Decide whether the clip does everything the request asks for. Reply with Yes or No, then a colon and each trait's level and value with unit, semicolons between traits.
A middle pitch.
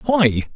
Yes: medium, 165 Hz